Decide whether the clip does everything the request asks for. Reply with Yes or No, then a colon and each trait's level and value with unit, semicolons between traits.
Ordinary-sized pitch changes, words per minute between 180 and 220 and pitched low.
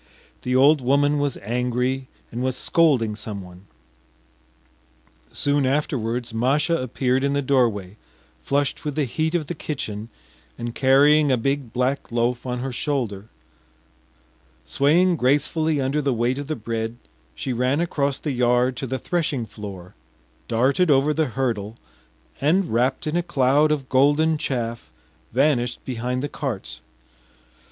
No: average, 3.4 semitones; average, 140 wpm; low, 130 Hz